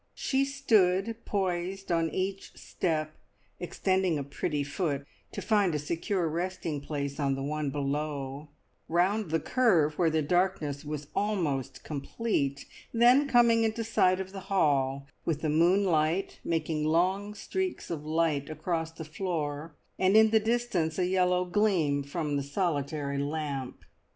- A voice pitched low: No, medium, 165 Hz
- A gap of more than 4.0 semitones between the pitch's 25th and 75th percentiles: Yes, average, 4.6 semitones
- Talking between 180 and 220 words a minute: No, average, 145 wpm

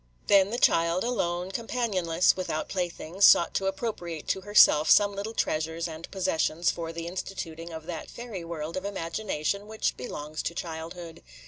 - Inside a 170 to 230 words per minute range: No, average, 155 wpm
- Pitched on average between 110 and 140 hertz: No, medium, 175 Hz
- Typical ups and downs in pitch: Yes, average, 3.2 semitones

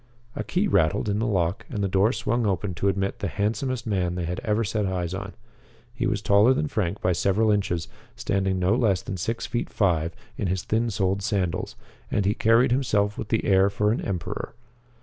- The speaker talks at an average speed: No, fast, 210 wpm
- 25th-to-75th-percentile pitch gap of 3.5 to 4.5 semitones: No, average, 3.0 semitones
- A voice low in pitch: Yes, low, 100 Hz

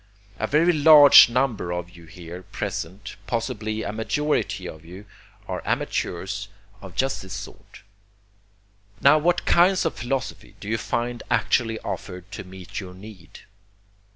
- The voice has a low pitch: Yes, low, 110 Hz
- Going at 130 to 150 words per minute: Yes, average, 140 wpm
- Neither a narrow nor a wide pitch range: No, wide, 6.7 semitones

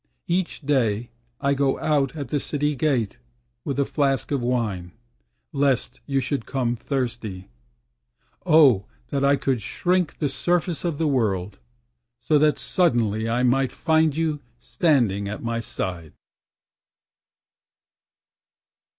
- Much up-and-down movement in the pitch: No, average, 4.3 semitones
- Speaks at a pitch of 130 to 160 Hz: Yes, low, 135 Hz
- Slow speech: Yes, slow, 125 wpm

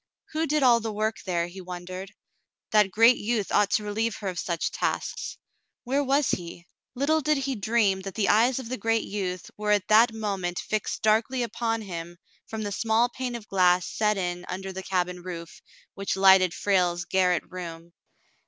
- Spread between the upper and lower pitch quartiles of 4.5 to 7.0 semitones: No, average, 3.9 semitones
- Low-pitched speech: No, high, 205 Hz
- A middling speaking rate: Yes, average, 185 wpm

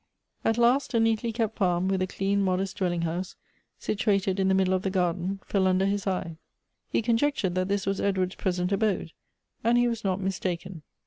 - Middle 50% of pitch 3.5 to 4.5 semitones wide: No, narrow, 2.4 semitones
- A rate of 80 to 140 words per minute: No, average, 200 wpm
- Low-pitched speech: No, high, 195 Hz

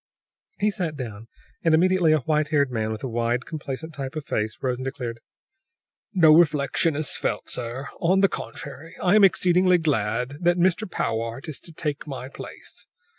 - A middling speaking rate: Yes, average, 175 wpm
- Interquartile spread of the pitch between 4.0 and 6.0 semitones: Yes, average, 5.2 semitones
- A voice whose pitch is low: No, medium, 150 Hz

